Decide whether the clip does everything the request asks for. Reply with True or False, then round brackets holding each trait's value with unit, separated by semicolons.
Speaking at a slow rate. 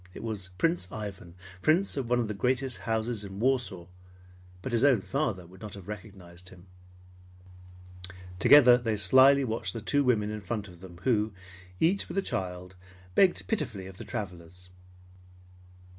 False (160 wpm)